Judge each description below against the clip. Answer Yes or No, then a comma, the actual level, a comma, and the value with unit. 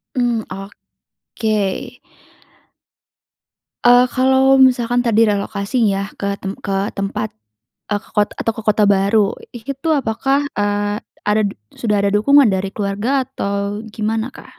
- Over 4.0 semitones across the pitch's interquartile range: No, average, 3.5 semitones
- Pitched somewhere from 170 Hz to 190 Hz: No, high, 215 Hz